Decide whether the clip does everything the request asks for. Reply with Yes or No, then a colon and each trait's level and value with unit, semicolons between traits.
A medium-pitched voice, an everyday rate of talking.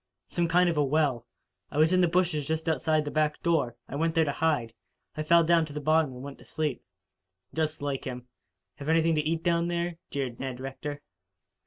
No: medium, 155 Hz; fast, 215 wpm